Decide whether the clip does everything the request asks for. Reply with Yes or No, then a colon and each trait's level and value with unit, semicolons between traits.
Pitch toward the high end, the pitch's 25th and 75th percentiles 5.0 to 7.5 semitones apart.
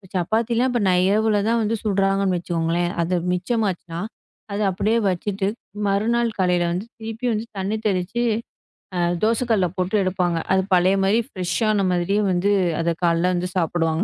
No: high, 195 Hz; average, 3.4 semitones